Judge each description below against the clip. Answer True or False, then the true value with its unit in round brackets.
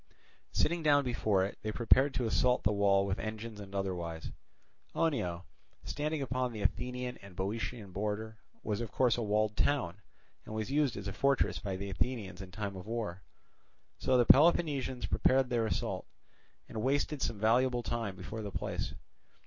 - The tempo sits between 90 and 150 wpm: False (175 wpm)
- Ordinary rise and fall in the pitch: True (4.2 semitones)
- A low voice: True (110 Hz)